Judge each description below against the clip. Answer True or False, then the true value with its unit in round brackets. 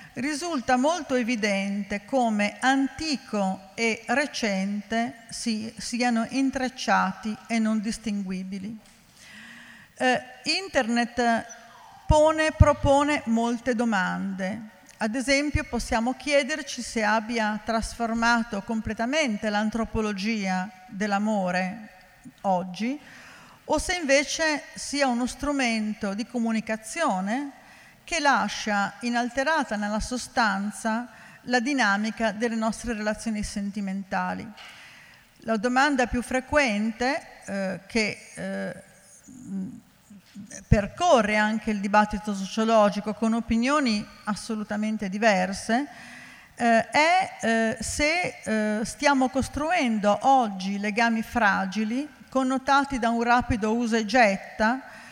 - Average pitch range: True (3.6 semitones)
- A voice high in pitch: True (230 Hz)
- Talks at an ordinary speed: False (90 wpm)